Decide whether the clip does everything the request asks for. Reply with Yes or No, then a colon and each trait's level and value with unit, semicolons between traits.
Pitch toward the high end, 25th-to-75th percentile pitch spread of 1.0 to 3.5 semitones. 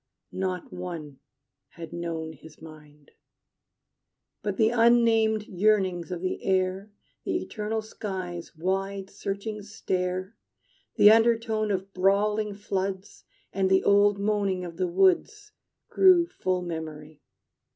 Yes: high, 195 Hz; average, 3.0 semitones